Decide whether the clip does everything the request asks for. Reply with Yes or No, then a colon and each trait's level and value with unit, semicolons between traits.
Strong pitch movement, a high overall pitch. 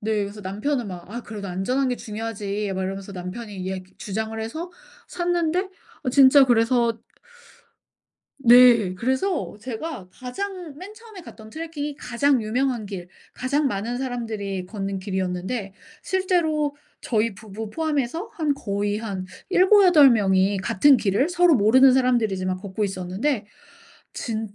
Yes: wide, 6.2 semitones; high, 230 Hz